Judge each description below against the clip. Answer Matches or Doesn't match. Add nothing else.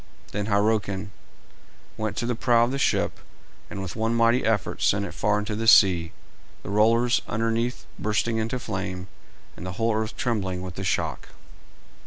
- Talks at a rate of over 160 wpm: Matches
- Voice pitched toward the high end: Doesn't match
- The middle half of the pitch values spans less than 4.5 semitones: Matches